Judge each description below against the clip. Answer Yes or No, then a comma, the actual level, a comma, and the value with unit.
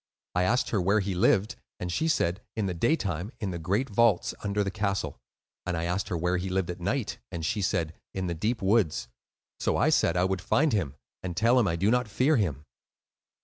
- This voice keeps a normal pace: No, fast, 230 wpm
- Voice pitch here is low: Yes, very low, 95 Hz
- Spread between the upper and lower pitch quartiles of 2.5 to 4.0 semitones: Yes, average, 3.7 semitones